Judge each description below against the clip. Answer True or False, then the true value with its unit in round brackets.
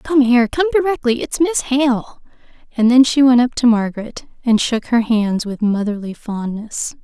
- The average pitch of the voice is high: True (240 Hz)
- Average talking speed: True (180 wpm)